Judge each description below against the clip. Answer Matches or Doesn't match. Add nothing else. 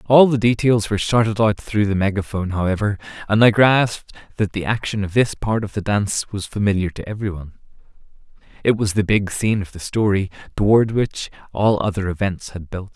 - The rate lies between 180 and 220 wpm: Matches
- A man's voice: Matches